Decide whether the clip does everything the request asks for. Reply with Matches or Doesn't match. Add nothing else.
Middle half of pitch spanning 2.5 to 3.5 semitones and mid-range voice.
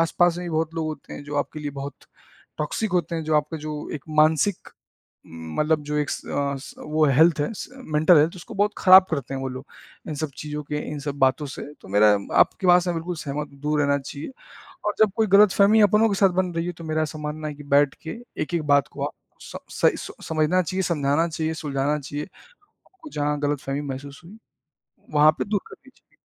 Matches